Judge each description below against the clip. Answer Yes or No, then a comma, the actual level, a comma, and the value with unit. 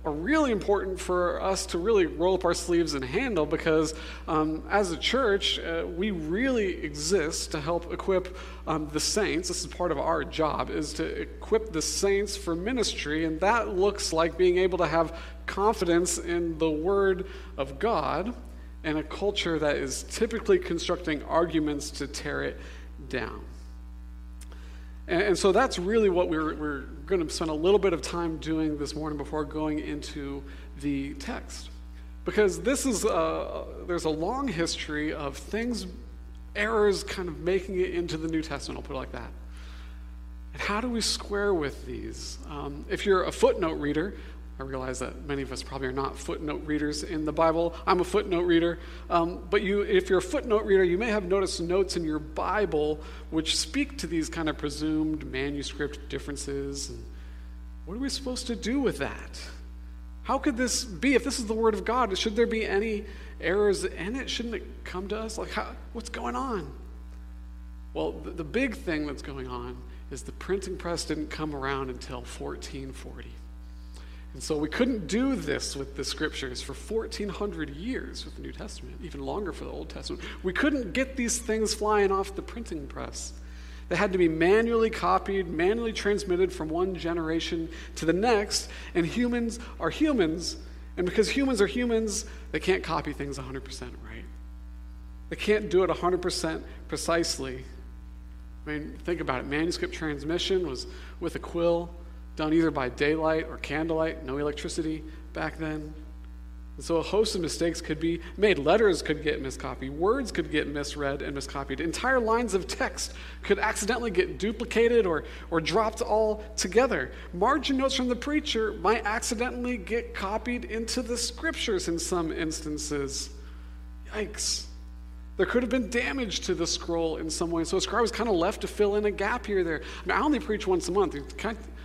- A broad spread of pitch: Yes, wide, 7.9 semitones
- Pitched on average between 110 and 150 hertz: No, medium, 165 Hz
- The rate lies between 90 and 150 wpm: No, average, 180 wpm